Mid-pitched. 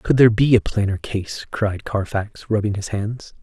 No: low, 105 Hz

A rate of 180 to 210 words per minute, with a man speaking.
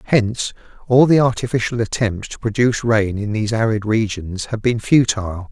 No: average, 165 wpm; male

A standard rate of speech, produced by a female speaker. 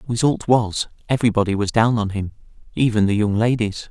No: average, 155 wpm; male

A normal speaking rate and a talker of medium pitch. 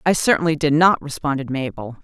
Yes: average, 175 wpm; medium, 145 Hz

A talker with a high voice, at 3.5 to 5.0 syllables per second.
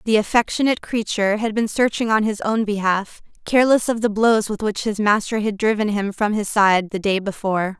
No: high, 210 Hz; 5.6 syllables/s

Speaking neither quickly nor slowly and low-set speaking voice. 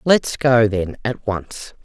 Yes: average, 165 wpm; low, 115 Hz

